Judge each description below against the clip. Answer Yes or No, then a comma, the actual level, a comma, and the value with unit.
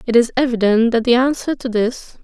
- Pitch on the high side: Yes, high, 240 Hz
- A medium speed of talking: No, fast, 215 wpm